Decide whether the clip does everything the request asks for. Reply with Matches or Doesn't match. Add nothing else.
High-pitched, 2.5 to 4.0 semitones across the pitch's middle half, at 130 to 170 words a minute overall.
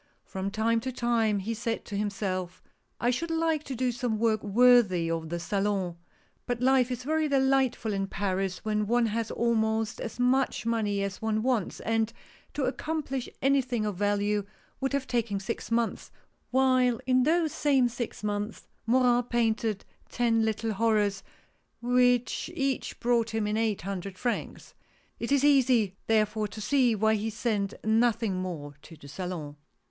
Matches